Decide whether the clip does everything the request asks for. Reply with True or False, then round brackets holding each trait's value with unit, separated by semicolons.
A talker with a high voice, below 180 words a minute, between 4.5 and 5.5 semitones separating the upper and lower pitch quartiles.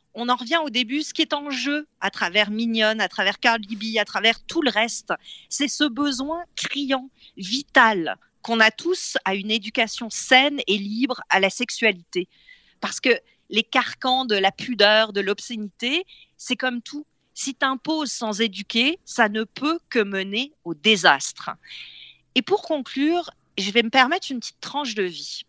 True (240 Hz; 170 wpm; 4.9 semitones)